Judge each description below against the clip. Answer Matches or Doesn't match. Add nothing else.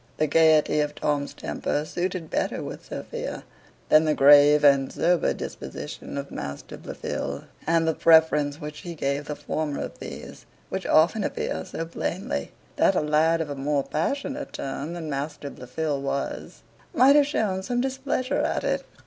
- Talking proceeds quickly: Doesn't match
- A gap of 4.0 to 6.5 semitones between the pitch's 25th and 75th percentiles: Doesn't match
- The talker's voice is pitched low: Doesn't match